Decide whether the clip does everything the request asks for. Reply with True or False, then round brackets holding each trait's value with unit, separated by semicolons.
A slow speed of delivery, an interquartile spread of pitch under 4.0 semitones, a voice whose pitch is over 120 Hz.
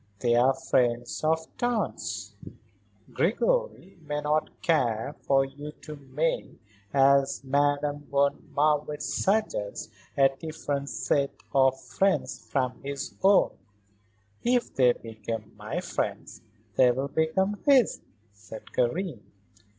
True (110 wpm; 3.4 semitones; 140 Hz)